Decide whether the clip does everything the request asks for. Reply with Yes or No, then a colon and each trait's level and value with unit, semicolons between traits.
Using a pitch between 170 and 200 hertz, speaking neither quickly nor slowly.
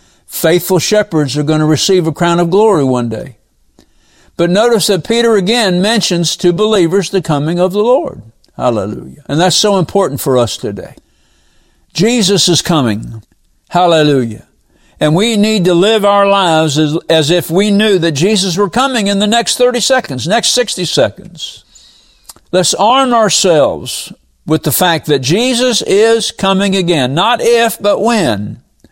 Yes: medium, 185 Hz; average, 160 wpm